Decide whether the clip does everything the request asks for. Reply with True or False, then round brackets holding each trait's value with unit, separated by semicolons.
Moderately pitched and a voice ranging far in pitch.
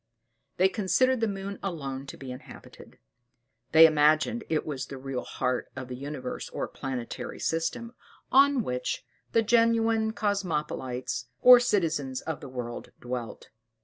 True (155 Hz; 8.9 semitones)